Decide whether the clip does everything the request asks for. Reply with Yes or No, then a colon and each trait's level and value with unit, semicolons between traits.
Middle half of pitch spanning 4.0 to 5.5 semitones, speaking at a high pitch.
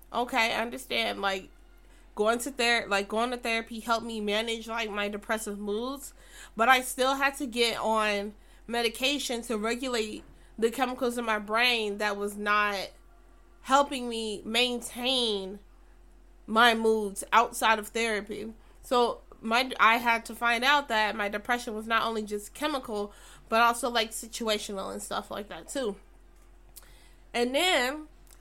No: narrow, 2.4 semitones; high, 225 Hz